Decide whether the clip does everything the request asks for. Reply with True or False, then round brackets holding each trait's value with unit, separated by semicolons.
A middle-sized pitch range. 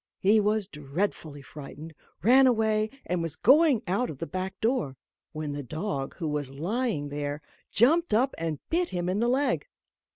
False (7.8 semitones)